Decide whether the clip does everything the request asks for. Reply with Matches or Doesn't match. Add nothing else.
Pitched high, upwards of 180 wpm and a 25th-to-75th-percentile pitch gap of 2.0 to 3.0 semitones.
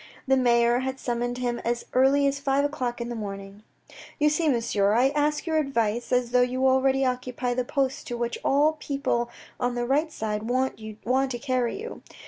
Matches